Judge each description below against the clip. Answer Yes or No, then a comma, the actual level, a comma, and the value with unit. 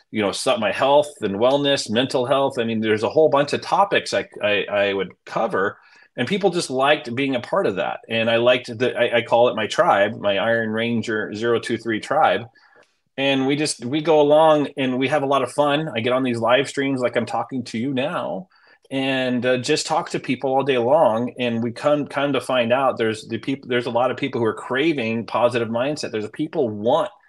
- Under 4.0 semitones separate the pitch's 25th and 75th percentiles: Yes, average, 3.3 semitones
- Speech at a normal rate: No, fast, 225 wpm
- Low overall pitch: Yes, low, 125 Hz